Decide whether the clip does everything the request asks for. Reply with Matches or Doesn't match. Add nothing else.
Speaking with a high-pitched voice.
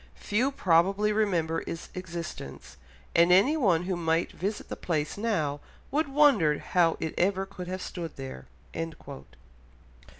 Doesn't match